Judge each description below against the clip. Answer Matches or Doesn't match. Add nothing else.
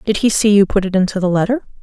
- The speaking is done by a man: Doesn't match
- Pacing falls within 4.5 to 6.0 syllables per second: Doesn't match